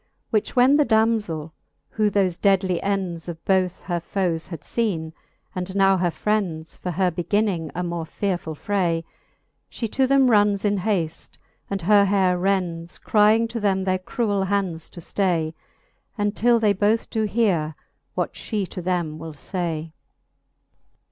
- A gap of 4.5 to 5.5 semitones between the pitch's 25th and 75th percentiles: No, average, 3.4 semitones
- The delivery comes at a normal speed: Yes, average, 155 wpm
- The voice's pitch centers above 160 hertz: Yes, high, 190 Hz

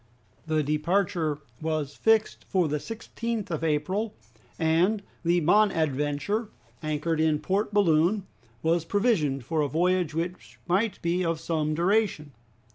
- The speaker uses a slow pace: Yes, slow, 125 wpm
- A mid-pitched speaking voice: Yes, medium, 170 Hz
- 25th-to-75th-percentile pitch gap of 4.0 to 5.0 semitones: Yes, average, 4.6 semitones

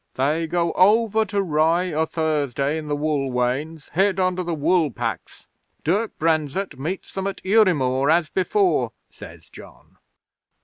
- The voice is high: No, medium, 160 Hz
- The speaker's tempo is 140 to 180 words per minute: Yes, average, 145 wpm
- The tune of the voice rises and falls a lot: No, average, 4.3 semitones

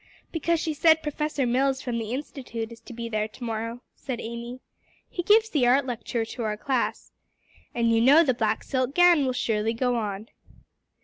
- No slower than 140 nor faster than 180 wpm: No, average, 190 wpm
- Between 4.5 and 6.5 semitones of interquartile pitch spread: No, average, 3.7 semitones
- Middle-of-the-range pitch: No, high, 245 Hz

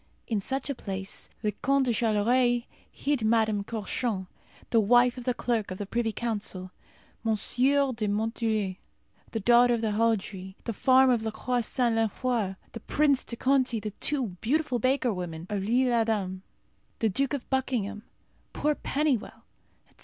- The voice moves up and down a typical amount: Yes, average, 3.4 semitones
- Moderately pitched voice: No, high, 230 Hz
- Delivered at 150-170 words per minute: Yes, average, 160 wpm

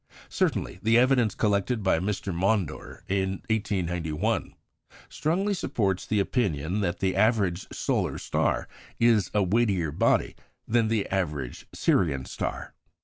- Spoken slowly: Yes, slow, 125 wpm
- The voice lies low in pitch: Yes, low, 100 Hz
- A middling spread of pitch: Yes, average, 4.0 semitones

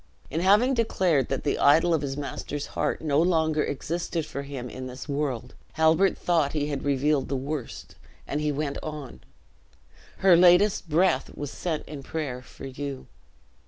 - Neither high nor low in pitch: Yes, medium, 150 Hz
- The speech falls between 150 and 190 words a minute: Yes, average, 165 wpm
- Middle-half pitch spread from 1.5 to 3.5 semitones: Yes, average, 3.0 semitones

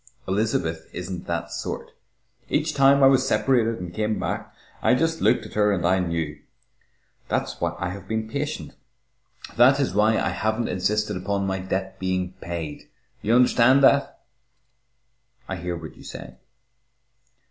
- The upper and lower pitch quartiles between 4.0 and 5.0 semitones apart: Yes, average, 4.7 semitones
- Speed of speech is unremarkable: Yes, average, 155 wpm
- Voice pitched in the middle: No, low, 100 Hz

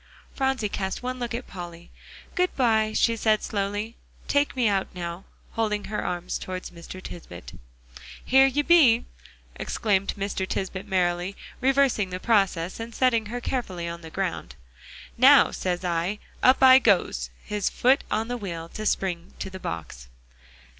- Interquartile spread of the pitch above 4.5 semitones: Yes, average, 5.2 semitones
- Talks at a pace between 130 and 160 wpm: Yes, average, 155 wpm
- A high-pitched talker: Yes, high, 205 Hz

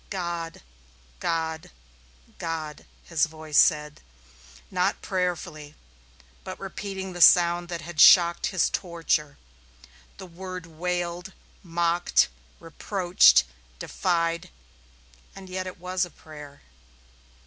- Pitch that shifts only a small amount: Yes, narrow, 2.1 semitones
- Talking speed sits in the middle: No, slow, 100 wpm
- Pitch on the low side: No, medium, 170 Hz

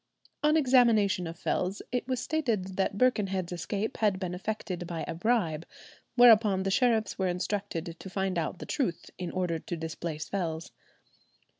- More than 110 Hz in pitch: Yes, high, 190 Hz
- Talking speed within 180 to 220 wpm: No, average, 160 wpm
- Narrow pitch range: No, average, 4.2 semitones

